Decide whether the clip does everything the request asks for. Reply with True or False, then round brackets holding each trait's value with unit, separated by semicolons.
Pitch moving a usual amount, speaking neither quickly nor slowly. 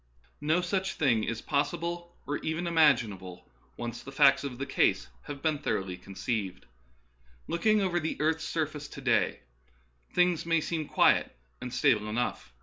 False (6.0 semitones; 155 wpm)